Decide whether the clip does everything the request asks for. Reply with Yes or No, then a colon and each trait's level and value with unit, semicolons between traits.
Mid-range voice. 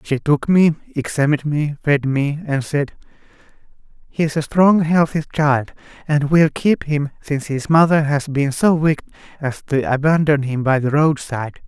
Yes: medium, 145 Hz